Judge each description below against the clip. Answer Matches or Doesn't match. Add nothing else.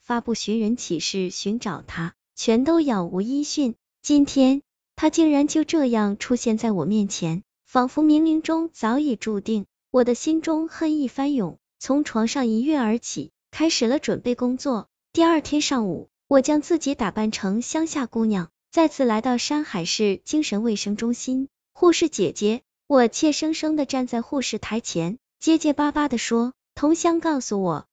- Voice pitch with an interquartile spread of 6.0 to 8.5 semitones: Doesn't match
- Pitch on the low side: Doesn't match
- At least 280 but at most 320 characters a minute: Doesn't match